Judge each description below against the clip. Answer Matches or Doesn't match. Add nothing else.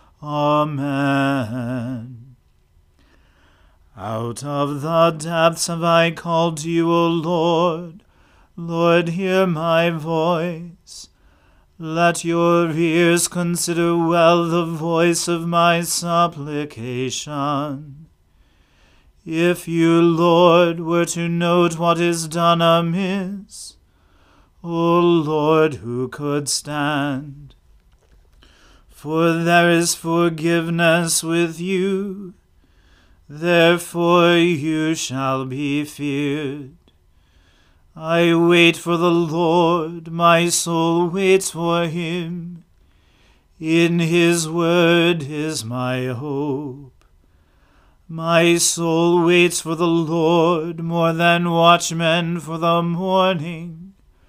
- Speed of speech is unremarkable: Doesn't match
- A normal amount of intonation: Matches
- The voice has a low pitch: Doesn't match